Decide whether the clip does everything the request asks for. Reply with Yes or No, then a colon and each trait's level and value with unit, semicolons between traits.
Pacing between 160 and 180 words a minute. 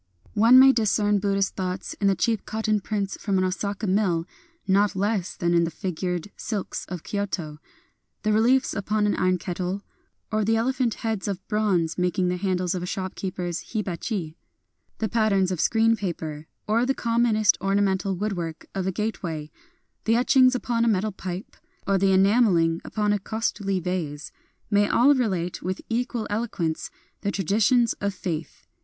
Yes: average, 175 wpm